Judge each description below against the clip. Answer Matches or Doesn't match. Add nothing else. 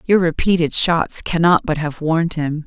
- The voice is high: Doesn't match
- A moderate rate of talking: Matches